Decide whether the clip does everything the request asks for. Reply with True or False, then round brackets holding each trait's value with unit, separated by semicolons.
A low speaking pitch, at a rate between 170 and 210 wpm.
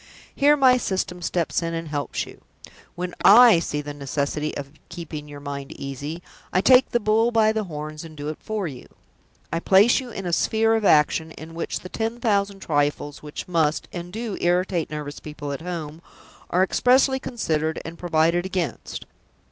False (170 Hz; 180 wpm)